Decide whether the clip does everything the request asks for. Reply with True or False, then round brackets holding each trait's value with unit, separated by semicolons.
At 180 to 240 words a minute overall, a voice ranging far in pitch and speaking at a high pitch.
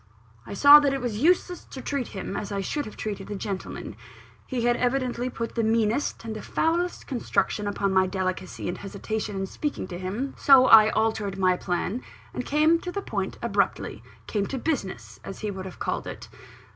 True (195 wpm; 5.7 semitones; 220 Hz)